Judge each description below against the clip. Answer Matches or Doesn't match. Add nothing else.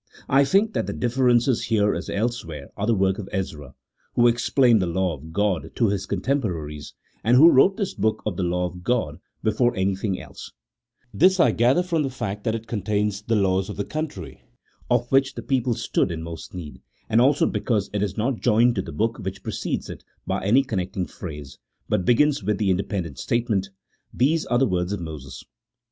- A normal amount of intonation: Matches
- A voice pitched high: Doesn't match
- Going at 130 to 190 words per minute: Doesn't match